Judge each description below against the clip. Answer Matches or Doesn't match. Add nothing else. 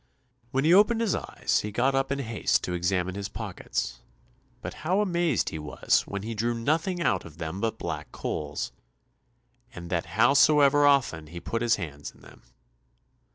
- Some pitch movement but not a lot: Doesn't match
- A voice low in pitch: Matches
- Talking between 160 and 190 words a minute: Matches